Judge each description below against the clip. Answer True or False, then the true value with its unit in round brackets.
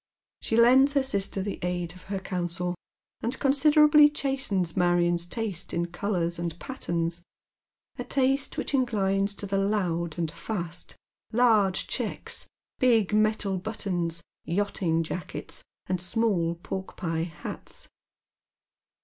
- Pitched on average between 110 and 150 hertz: False (195 Hz)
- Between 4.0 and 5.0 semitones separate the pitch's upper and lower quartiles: True (4.6 semitones)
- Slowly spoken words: True (130 wpm)